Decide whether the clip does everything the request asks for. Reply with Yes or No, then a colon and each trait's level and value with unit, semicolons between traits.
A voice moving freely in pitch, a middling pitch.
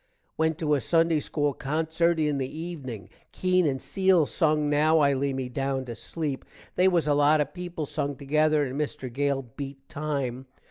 No: average, 2.8 semitones; medium, 150 Hz